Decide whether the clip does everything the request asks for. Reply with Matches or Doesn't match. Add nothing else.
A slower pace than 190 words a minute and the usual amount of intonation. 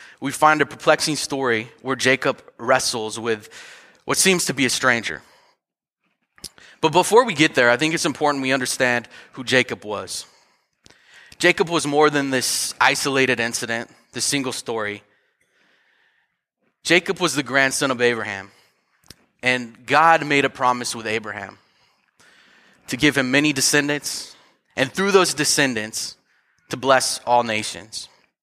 Matches